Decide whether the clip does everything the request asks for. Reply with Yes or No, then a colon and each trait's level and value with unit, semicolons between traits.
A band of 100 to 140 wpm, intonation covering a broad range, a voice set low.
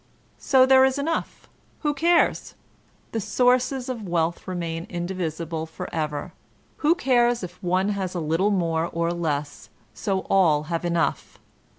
No: slow, 135 wpm; wide, 6.9 semitones; medium, 180 Hz